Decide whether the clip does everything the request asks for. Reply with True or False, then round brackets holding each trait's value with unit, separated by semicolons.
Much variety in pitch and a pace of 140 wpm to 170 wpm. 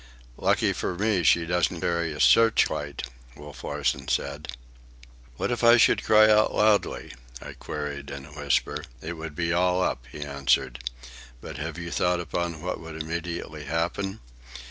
False (3.4 semitones; 160 wpm)